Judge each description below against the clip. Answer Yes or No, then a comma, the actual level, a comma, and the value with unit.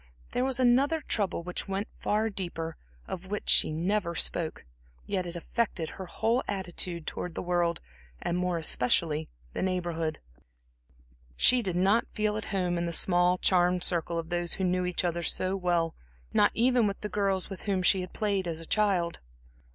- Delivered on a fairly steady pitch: No, average, 3.0 semitones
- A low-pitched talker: No, medium, 180 Hz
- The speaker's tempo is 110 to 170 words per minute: No, average, 180 wpm